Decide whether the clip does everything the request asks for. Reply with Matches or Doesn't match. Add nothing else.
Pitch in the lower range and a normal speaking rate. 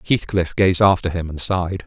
Matches